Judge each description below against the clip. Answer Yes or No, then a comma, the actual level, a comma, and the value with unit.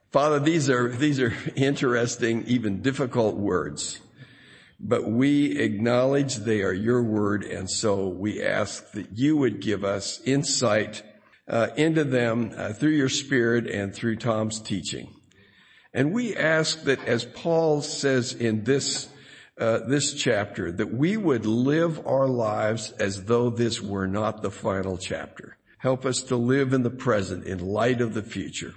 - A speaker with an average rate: Yes, average, 155 wpm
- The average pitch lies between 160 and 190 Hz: No, low, 120 Hz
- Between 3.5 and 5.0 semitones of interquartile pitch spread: Yes, average, 4.2 semitones